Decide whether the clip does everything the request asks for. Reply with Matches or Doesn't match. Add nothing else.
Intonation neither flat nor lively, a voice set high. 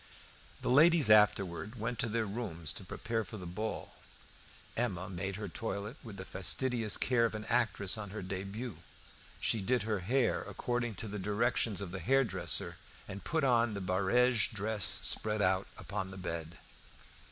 Doesn't match